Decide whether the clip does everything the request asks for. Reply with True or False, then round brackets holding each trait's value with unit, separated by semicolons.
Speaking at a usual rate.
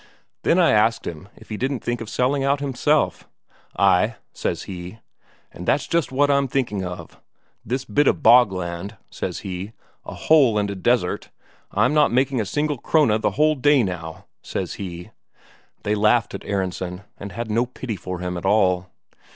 True (175 wpm)